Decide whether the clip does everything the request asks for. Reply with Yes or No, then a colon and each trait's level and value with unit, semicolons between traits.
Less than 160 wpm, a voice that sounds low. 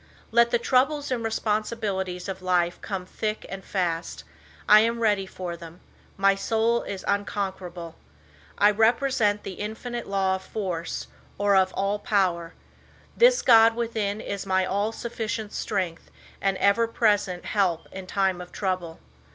No: average, 150 wpm; high, 200 Hz